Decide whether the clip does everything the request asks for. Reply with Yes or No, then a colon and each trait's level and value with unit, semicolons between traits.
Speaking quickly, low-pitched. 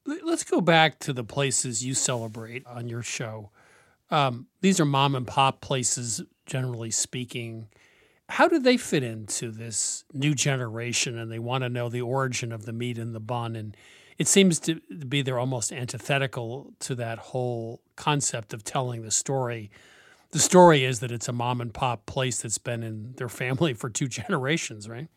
No: average, 180 wpm; low, 125 Hz